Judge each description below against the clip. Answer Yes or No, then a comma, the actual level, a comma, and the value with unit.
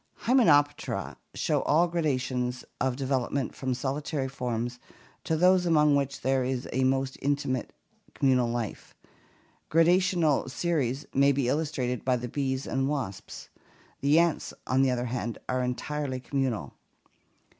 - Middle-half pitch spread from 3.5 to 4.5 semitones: No, average, 2.8 semitones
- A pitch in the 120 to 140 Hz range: Yes, low, 135 Hz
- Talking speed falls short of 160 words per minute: Yes, slow, 135 wpm